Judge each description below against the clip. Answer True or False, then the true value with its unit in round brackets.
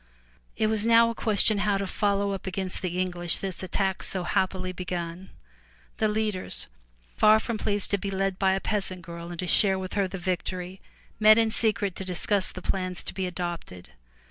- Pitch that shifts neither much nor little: False (2.2 semitones)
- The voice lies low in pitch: False (190 Hz)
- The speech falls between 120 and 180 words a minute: False (195 wpm)